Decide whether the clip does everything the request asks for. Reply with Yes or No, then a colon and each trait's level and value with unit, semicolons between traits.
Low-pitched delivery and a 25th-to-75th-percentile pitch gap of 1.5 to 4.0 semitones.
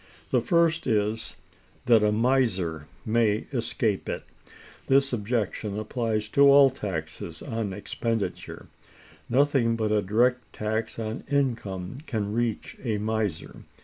Yes: low, 110 Hz; average, 3.1 semitones